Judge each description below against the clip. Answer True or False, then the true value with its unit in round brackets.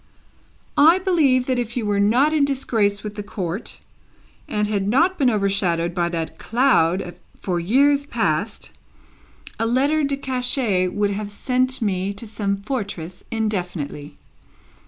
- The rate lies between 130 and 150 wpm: True (140 wpm)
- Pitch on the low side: False (210 Hz)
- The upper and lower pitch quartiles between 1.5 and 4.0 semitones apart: False (4.9 semitones)